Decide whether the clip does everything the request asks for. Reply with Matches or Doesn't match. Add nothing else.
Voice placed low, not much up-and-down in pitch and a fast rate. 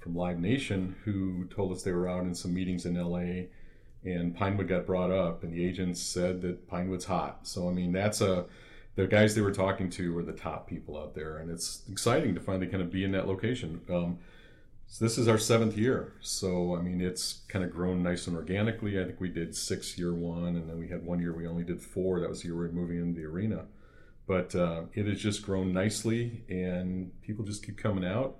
Matches